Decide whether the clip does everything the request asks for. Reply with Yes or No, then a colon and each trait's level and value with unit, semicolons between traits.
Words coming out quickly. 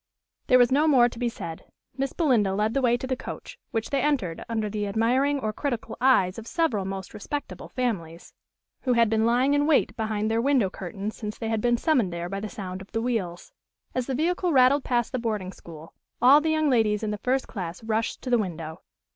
Yes: fast, 220 wpm